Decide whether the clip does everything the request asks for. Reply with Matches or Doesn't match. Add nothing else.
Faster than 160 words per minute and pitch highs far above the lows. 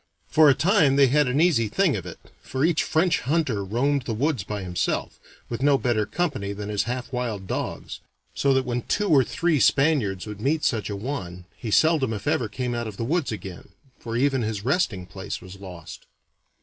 Matches